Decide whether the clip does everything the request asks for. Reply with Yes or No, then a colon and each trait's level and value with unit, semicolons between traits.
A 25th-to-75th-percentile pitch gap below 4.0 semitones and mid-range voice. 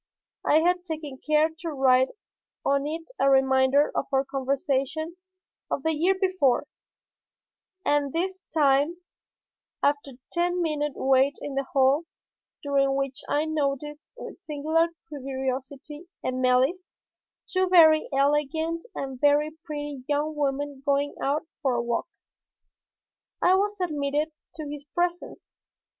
No: average, 2.7 semitones; very high, 290 Hz